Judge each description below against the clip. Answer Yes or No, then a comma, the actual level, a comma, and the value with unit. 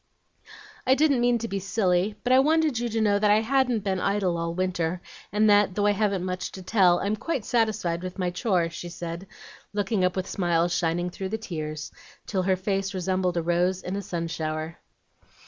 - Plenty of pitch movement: No, average, 3.4 semitones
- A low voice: No, high, 190 Hz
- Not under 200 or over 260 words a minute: Yes, fast, 205 wpm